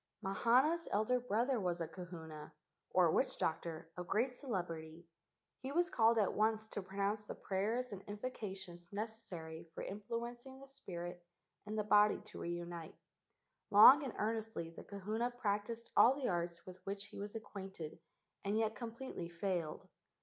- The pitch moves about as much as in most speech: Yes, average, 4.8 semitones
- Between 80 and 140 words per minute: No, average, 155 wpm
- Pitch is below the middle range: No, high, 205 Hz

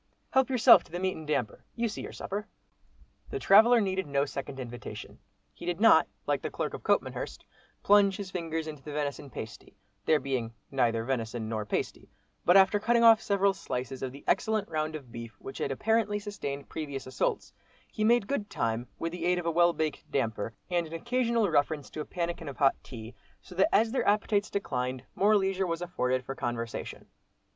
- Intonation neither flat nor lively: No, wide, 7.2 semitones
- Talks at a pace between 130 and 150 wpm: No, average, 195 wpm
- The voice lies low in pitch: No, medium, 165 Hz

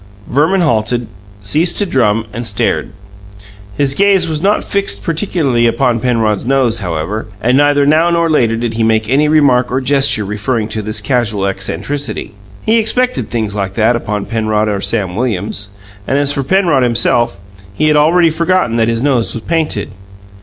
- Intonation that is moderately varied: No, wide, 5.7 semitones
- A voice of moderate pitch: No, low, 125 Hz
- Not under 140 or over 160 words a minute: No, average, 170 wpm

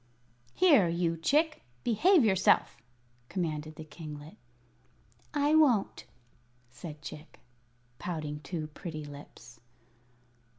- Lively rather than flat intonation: Yes, wide, 7.3 semitones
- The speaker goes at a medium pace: No, slow, 90 wpm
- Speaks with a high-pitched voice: No, medium, 165 Hz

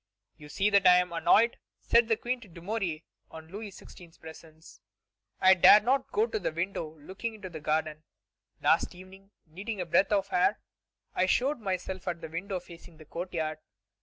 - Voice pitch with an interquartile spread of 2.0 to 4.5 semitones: Yes, average, 4.0 semitones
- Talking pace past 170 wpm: Yes, average, 180 wpm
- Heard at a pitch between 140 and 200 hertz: Yes, medium, 185 Hz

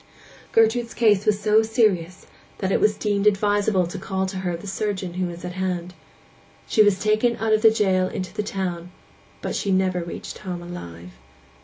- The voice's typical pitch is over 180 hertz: Yes, high, 190 Hz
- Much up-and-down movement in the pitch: No, average, 2.8 semitones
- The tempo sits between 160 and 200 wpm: Yes, average, 185 wpm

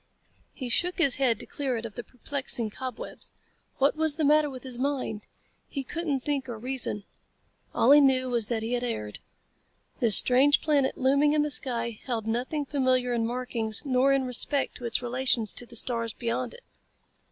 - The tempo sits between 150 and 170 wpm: No, average, 185 wpm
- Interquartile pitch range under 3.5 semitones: Yes, average, 3.1 semitones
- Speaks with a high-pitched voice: Yes, very high, 255 Hz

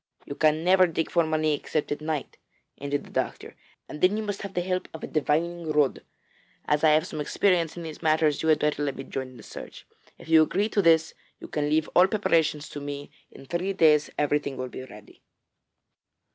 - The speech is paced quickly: Yes, fast, 215 wpm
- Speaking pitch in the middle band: Yes, medium, 155 Hz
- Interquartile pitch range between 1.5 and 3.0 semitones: Yes, average, 2.7 semitones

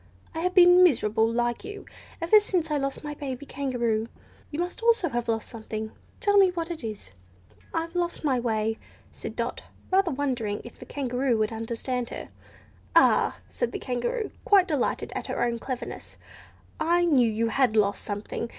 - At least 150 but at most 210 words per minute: Yes, average, 175 wpm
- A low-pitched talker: No, very high, 260 Hz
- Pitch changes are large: Yes, wide, 7.1 semitones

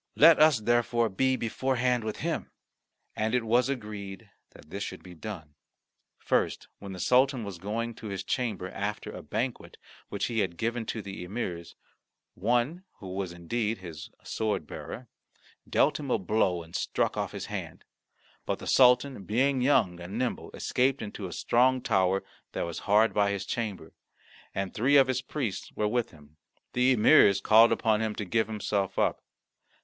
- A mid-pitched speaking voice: No, low, 110 Hz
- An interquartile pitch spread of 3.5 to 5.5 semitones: Yes, average, 4.2 semitones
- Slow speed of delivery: No, average, 175 wpm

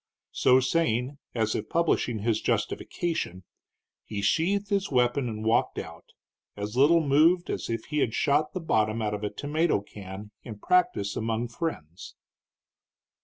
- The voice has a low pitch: Yes, low, 120 Hz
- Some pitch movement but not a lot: No, wide, 6.9 semitones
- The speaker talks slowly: No, average, 150 wpm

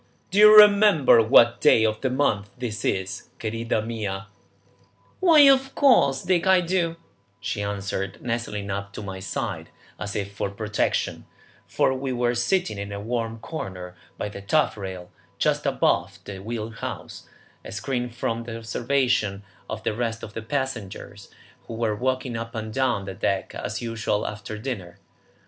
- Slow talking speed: No, average, 160 wpm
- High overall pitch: No, low, 115 Hz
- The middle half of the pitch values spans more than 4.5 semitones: No, average, 4.2 semitones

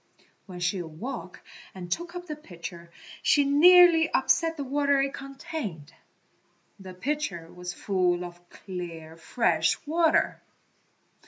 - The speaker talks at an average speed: No, slow, 120 wpm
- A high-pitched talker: Yes, high, 195 Hz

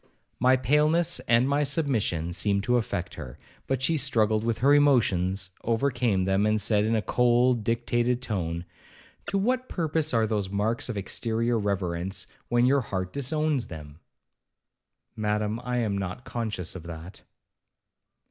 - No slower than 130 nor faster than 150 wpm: Yes, average, 145 wpm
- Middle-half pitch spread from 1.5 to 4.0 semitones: No, average, 4.6 semitones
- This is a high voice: No, low, 115 Hz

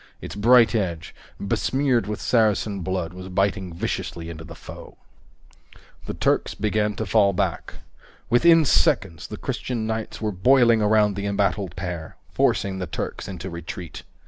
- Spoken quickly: No, average, 145 wpm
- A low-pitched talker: Yes, low, 100 Hz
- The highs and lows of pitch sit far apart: No, average, 3.6 semitones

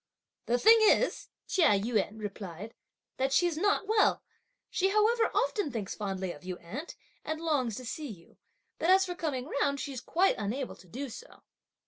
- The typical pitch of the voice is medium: No, very high, 270 Hz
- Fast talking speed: No, average, 170 wpm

